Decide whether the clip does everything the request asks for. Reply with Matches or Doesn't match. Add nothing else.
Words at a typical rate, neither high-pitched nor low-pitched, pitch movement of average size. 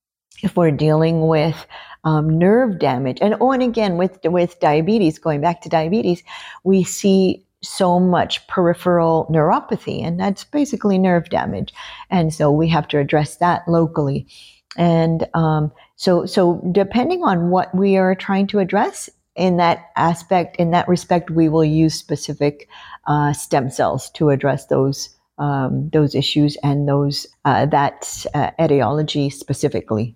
Matches